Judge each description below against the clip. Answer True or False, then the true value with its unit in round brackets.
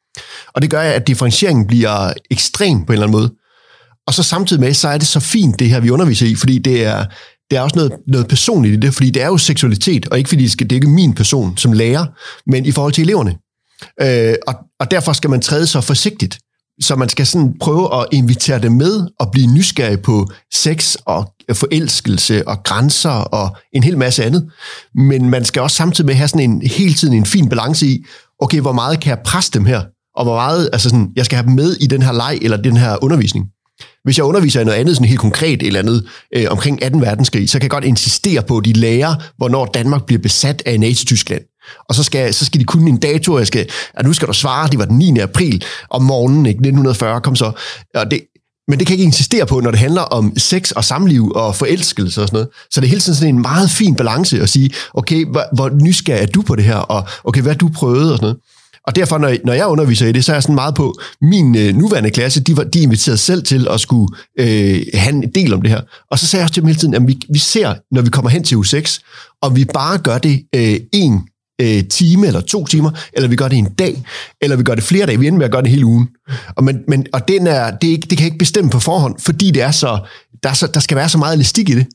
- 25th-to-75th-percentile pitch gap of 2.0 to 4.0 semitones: False (4.7 semitones)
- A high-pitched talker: False (135 Hz)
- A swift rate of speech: True (255 wpm)